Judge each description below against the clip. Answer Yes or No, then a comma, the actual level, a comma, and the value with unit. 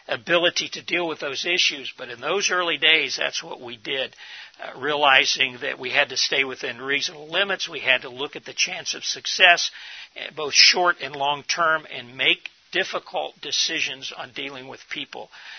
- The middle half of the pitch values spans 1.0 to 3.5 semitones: No, average, 4.1 semitones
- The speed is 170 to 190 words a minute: Yes, average, 175 wpm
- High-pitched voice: No, medium, 155 Hz